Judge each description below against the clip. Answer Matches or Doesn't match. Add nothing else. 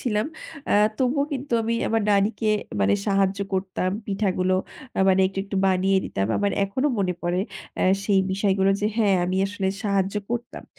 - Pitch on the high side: Matches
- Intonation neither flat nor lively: Doesn't match